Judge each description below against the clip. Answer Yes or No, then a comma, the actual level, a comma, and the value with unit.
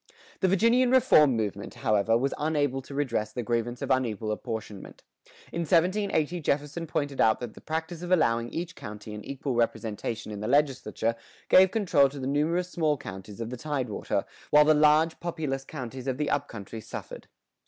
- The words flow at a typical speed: Yes, average, 175 wpm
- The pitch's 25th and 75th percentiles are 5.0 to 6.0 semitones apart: Yes, wide, 5.6 semitones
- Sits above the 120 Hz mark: Yes, medium, 140 Hz